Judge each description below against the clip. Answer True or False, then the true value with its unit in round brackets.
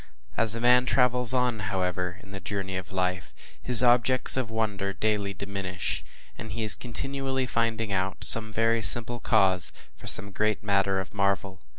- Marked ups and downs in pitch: False (3.4 semitones)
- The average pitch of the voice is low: True (105 Hz)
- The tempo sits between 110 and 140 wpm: False (170 wpm)